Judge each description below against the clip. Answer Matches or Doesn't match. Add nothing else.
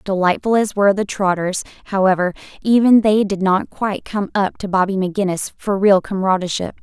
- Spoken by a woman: Matches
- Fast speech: Doesn't match